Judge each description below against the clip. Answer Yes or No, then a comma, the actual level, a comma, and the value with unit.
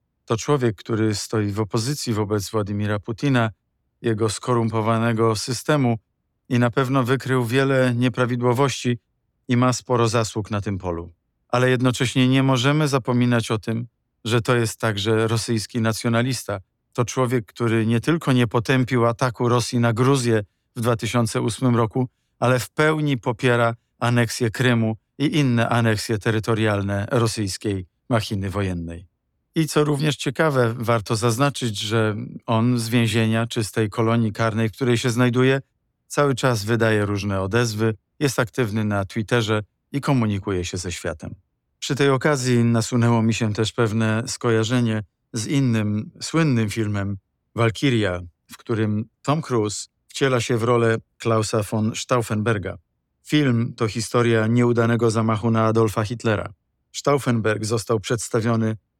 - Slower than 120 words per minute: No, average, 135 wpm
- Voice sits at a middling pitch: No, low, 115 Hz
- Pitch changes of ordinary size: No, narrow, 2.3 semitones